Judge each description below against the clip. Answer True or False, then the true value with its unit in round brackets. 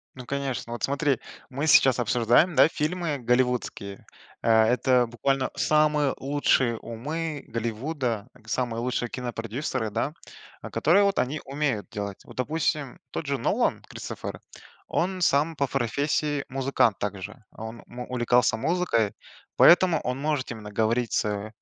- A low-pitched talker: True (130 Hz)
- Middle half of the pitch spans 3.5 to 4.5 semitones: True (4.2 semitones)